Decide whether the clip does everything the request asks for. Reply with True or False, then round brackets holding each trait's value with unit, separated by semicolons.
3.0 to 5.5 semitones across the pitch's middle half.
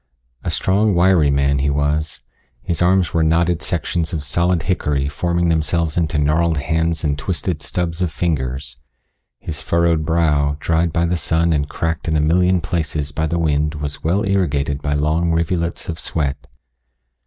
False (2.6 semitones)